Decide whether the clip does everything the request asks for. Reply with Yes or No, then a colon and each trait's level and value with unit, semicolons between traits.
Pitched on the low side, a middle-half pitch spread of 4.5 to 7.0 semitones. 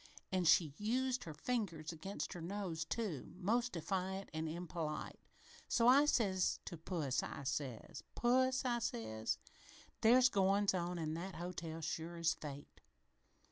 No: medium, 180 Hz; average, 5.1 semitones